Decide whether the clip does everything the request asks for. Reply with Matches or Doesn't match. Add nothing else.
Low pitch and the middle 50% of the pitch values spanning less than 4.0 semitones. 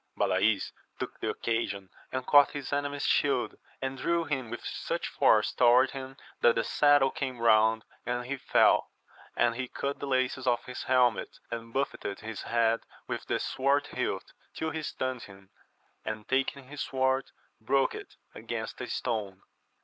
Matches